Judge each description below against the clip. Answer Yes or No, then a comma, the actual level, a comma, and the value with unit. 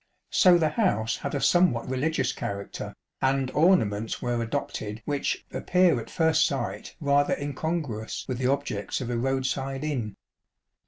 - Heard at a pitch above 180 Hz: No, low, 135 Hz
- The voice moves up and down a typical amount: Yes, average, 4.7 semitones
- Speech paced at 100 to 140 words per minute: No, average, 155 wpm